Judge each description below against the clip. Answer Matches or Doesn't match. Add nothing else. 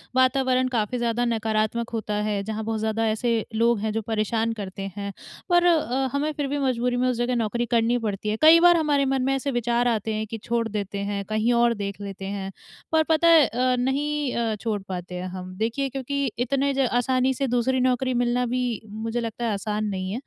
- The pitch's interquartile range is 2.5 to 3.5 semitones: Matches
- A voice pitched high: Matches